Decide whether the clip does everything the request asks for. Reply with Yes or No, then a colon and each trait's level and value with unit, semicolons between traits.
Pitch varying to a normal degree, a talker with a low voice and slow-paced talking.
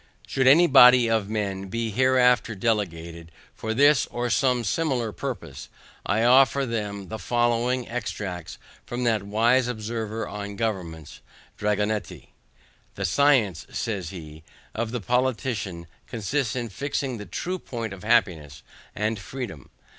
Yes: average, 3.6 semitones; low, 115 Hz; slow, 130 wpm